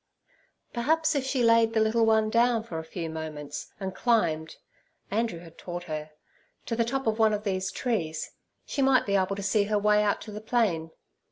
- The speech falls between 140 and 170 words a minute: No, average, 200 wpm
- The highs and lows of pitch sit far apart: No, average, 4.9 semitones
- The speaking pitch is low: No, high, 210 Hz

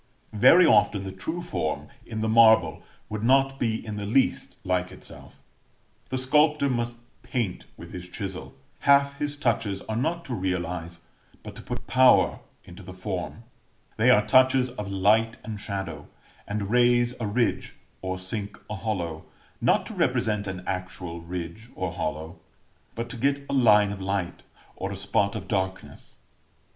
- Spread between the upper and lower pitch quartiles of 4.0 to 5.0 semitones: Yes, average, 4.6 semitones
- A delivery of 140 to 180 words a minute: Yes, average, 160 wpm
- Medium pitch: No, low, 105 Hz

